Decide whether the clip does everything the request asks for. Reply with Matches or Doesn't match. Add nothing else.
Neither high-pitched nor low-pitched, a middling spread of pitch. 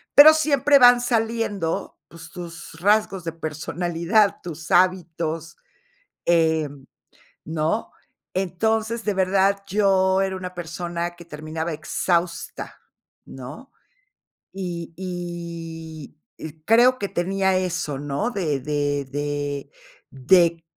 Matches